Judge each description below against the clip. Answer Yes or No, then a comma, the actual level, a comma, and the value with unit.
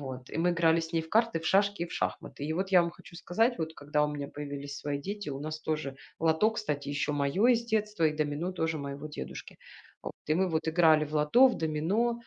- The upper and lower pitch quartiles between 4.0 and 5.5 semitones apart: Yes, average, 4.3 semitones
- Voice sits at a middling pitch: Yes, medium, 160 Hz